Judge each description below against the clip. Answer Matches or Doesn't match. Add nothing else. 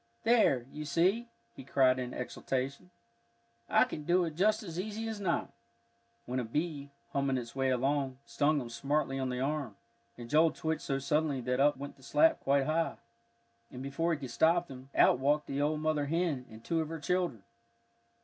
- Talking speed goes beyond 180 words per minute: Matches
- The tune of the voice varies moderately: Matches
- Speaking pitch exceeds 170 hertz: Doesn't match